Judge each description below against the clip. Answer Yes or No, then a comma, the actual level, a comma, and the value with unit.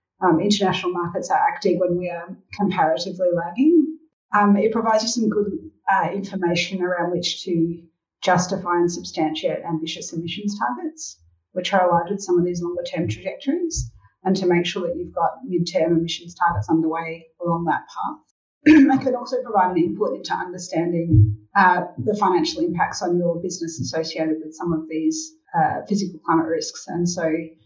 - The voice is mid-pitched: Yes, medium, 175 Hz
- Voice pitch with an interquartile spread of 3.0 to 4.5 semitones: Yes, average, 3.6 semitones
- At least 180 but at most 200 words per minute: No, average, 170 wpm